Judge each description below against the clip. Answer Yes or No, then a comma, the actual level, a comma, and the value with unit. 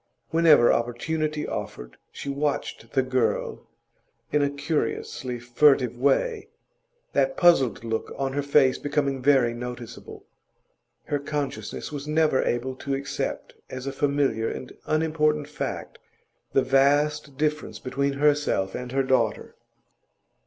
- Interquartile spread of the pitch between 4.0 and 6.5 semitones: No, average, 2.9 semitones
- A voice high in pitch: No, medium, 140 Hz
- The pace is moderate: No, slow, 125 wpm